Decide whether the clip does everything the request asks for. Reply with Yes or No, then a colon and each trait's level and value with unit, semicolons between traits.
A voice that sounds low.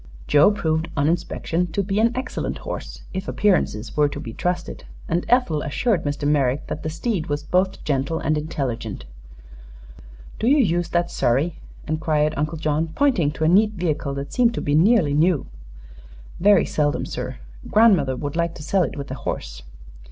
No: medium, 160 Hz